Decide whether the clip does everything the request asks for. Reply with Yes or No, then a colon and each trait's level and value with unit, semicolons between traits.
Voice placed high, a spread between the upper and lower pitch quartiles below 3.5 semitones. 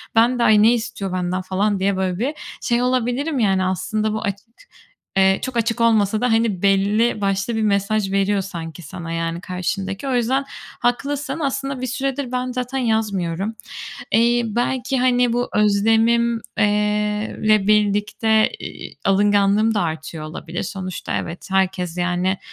No: high, 210 Hz; average, 3.8 semitones